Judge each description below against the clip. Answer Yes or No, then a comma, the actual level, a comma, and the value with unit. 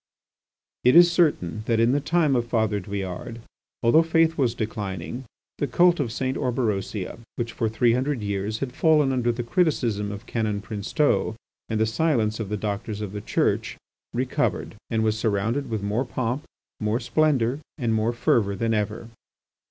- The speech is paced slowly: No, average, 165 wpm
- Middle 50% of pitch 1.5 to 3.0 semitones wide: No, average, 3.7 semitones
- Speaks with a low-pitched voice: Yes, low, 115 Hz